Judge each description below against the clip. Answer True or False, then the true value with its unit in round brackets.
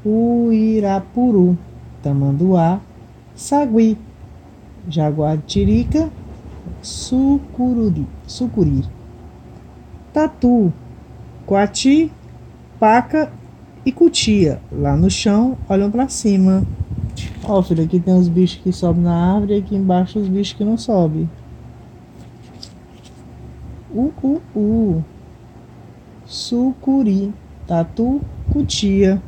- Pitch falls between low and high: False (200 Hz)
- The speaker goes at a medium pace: False (80 wpm)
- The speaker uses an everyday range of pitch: False (5.7 semitones)